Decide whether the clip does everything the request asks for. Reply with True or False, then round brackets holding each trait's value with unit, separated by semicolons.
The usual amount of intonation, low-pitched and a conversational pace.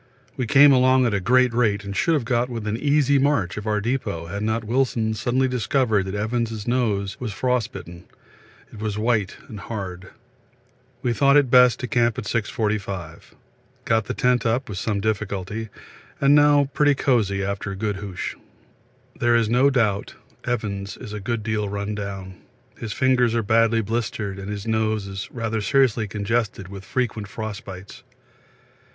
True (3.4 semitones; 110 Hz; 170 wpm)